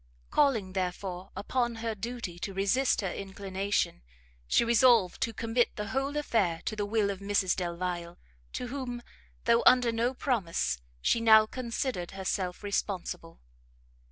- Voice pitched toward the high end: Yes, high, 210 Hz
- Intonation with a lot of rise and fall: No, average, 4.1 semitones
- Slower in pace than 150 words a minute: Yes, average, 140 wpm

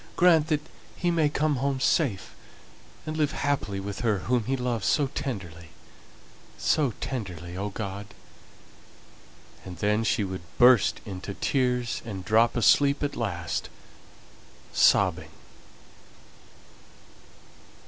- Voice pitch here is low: Yes, low, 115 Hz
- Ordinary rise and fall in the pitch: No, wide, 6.2 semitones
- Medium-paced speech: No, slow, 115 wpm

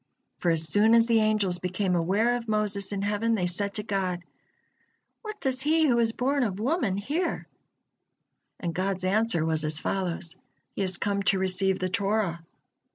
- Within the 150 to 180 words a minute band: Yes, average, 175 wpm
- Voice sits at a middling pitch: No, high, 200 Hz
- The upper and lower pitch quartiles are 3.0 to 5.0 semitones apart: Yes, average, 3.7 semitones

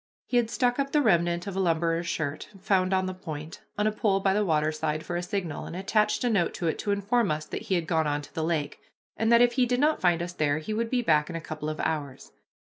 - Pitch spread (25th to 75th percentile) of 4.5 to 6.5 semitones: Yes, average, 5.2 semitones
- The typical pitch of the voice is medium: Yes, medium, 180 Hz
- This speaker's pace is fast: Yes, fast, 270 wpm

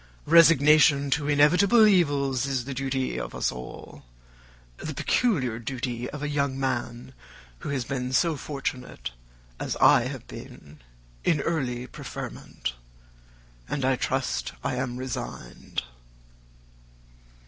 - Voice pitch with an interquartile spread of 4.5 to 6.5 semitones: No, average, 3.0 semitones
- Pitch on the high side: No, low, 135 Hz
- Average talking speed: No, slow, 120 wpm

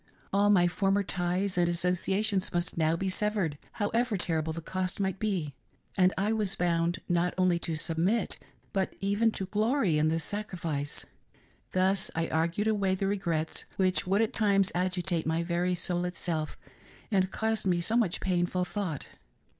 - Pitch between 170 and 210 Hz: Yes, medium, 185 Hz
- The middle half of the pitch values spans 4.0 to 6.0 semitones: No, average, 2.7 semitones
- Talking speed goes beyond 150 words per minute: Yes, average, 160 wpm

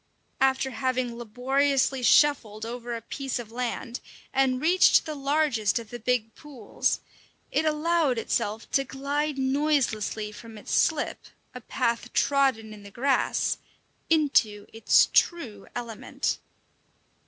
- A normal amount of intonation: Yes, average, 3.8 semitones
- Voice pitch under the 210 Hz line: No, very high, 255 Hz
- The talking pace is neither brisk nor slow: No, slow, 125 wpm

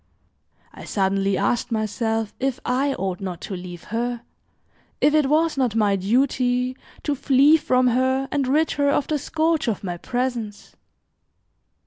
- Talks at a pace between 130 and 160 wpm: Yes, average, 150 wpm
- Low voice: No, very high, 250 Hz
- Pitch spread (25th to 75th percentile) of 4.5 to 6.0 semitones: Yes, average, 5.1 semitones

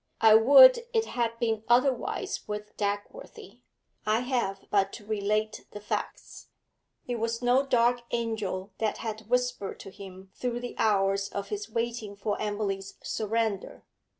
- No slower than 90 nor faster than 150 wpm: Yes, average, 145 wpm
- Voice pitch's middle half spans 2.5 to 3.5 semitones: Yes, average, 3.1 semitones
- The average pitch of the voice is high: Yes, high, 220 Hz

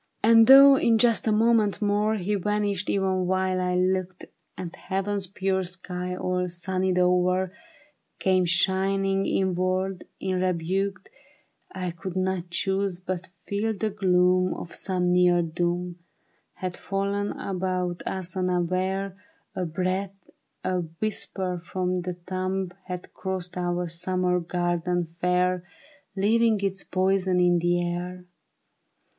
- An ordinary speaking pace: No, slow, 125 wpm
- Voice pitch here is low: No, medium, 185 Hz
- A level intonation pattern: Yes, narrow, 1.4 semitones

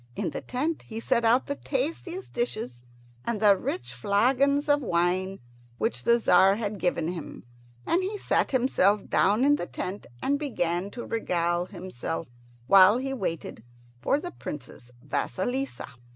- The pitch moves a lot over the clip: Yes, wide, 7.1 semitones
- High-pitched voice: Yes, high, 210 Hz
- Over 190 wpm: No, average, 150 wpm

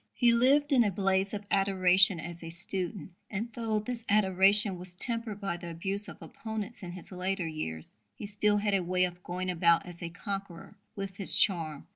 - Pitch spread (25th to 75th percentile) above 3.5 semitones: No, average, 2.8 semitones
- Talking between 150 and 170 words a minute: No, average, 195 wpm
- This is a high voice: Yes, high, 195 Hz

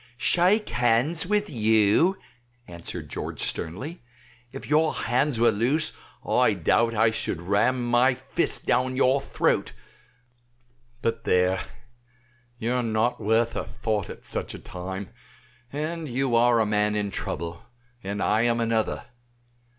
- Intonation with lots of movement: No, average, 4.1 semitones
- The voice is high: No, low, 115 Hz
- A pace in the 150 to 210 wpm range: No, slow, 135 wpm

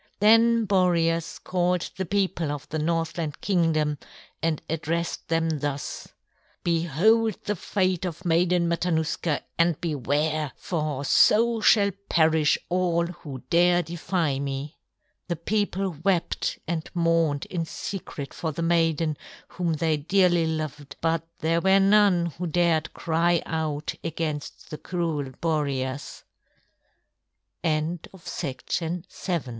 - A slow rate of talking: Yes, slow, 125 wpm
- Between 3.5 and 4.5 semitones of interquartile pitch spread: No, narrow, 2.4 semitones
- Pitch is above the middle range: No, medium, 165 Hz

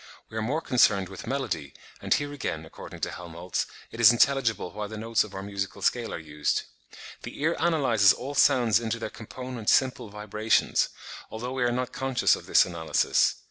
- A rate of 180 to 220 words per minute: Yes, average, 185 wpm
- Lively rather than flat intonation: No, average, 4.3 semitones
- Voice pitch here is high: No, low, 115 Hz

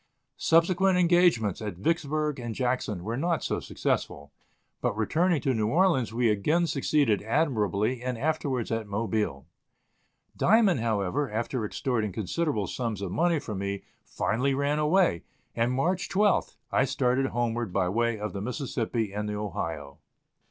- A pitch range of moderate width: No, wide, 6.3 semitones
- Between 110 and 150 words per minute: Yes, average, 145 wpm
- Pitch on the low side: Yes, low, 120 Hz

